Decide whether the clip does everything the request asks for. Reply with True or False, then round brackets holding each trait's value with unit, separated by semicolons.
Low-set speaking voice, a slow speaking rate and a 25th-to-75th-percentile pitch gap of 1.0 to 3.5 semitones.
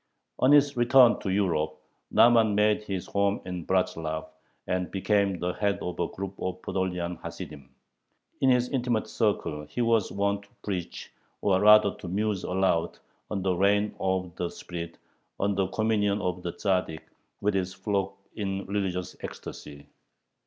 False (95 Hz; 155 wpm; 2.5 semitones)